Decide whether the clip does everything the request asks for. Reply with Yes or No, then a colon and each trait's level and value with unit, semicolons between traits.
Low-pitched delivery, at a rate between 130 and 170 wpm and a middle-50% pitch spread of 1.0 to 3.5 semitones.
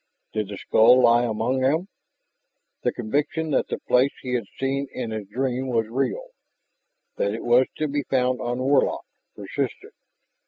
Yes: low, 125 Hz; average, 160 wpm; average, 2.9 semitones